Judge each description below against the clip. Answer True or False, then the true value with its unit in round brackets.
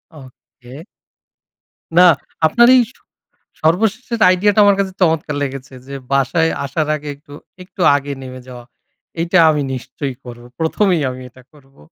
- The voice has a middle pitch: True (150 Hz)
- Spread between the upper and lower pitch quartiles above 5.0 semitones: True (5.5 semitones)